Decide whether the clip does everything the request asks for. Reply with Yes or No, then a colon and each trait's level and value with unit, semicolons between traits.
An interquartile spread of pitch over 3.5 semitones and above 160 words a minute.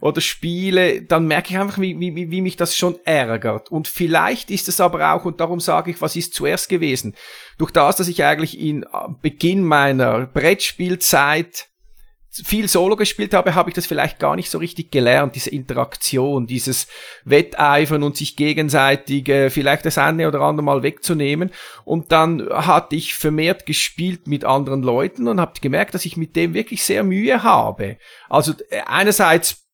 Yes: average, 3.9 semitones; average, 170 wpm